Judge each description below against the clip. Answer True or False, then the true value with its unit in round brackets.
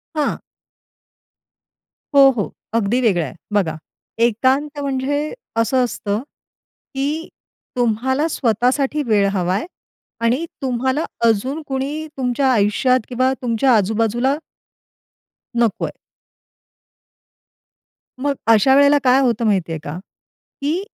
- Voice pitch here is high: True (250 Hz)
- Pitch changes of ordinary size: True (3.8 semitones)